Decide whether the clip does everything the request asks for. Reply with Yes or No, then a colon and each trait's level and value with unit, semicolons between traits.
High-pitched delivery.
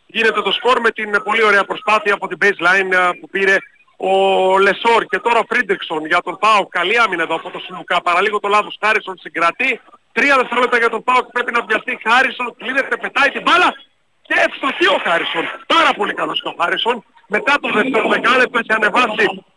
Yes: high, 215 Hz